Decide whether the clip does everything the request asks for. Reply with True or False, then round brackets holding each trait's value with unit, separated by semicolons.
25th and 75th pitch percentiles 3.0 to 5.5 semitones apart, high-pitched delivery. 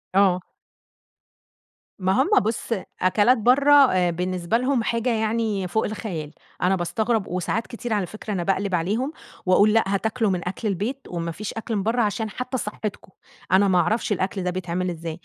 True (3.7 semitones; 205 Hz)